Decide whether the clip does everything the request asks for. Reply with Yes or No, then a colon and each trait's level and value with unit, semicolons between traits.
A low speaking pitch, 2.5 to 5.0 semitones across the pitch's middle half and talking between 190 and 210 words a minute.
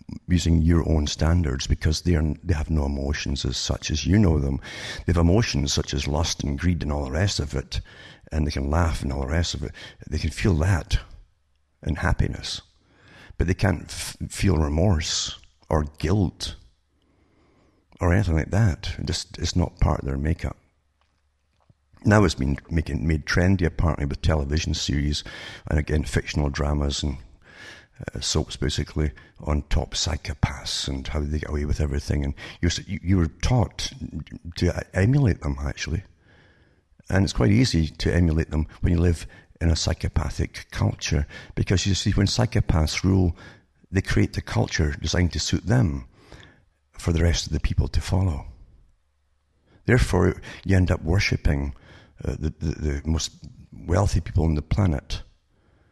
No: very low, 80 Hz; average, 3.7 semitones; average, 165 wpm